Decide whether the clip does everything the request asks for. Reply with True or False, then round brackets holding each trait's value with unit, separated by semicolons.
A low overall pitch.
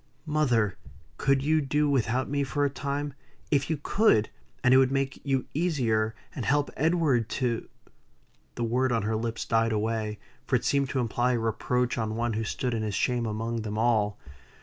True (125 Hz)